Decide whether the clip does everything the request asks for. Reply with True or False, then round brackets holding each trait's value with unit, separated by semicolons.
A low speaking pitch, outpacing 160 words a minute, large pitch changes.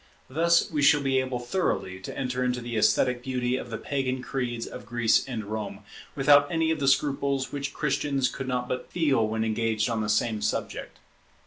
False (125 Hz; 195 wpm; 3.2 semitones)